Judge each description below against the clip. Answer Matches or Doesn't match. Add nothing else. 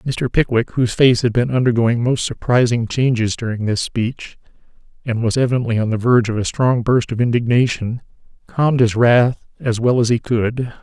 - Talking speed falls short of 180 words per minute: Doesn't match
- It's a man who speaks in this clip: Matches